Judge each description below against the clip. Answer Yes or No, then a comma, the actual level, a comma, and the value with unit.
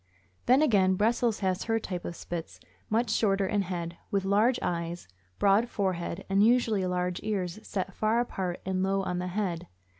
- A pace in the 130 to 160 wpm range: No, average, 175 wpm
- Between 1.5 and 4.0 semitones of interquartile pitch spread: Yes, average, 3.1 semitones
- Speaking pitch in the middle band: No, high, 195 Hz